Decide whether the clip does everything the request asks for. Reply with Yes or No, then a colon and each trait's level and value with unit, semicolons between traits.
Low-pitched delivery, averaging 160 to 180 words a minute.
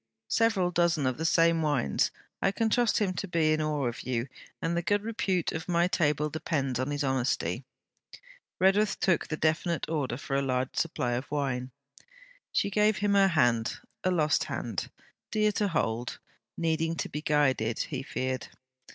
No: medium, 155 Hz; average, 175 wpm